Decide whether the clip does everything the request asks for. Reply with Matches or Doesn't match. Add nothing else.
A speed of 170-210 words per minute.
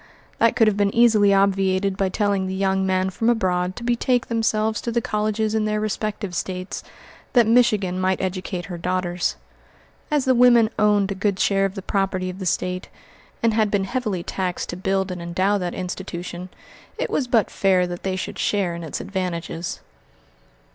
Matches